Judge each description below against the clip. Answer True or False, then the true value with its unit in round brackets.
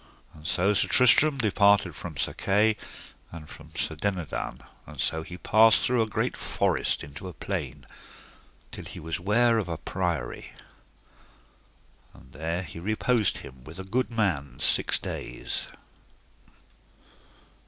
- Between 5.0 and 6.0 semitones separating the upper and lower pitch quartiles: True (5.3 semitones)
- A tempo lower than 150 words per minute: True (140 wpm)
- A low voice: True (95 Hz)